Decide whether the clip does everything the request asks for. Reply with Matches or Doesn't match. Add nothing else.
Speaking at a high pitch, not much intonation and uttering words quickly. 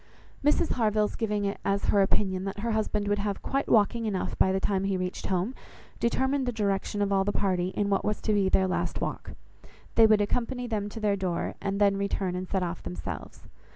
Matches